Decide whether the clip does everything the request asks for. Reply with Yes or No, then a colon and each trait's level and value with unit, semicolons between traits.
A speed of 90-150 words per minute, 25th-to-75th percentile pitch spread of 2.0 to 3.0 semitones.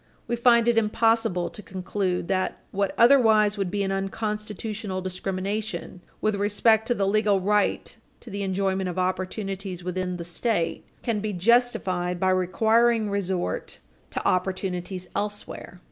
Yes: average, 140 wpm; narrow, 2.6 semitones